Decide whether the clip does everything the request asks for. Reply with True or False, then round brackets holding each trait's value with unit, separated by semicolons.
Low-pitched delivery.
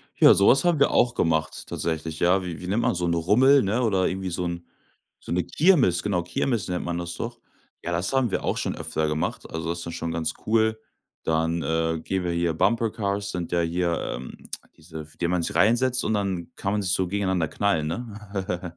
True (90 Hz)